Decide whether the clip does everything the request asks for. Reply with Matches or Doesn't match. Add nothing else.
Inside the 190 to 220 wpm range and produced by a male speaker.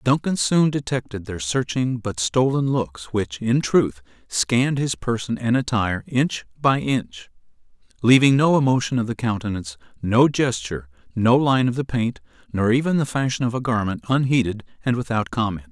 Doesn't match